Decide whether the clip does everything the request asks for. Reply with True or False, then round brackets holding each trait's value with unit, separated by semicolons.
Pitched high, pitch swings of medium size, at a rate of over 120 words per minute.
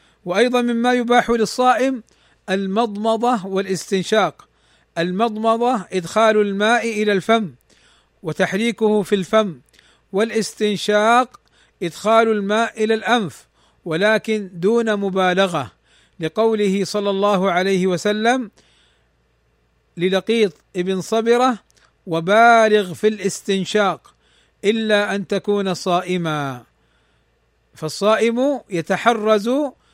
False (205 Hz; 3.5 semitones; 80 wpm)